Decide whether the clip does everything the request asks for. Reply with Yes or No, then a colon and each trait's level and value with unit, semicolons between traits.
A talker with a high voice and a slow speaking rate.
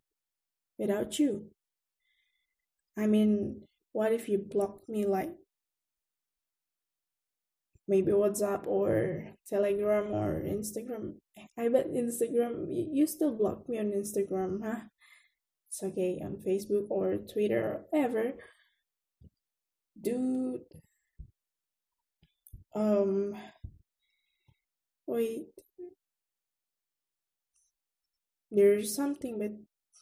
Yes: high, 220 Hz; slow, 80 wpm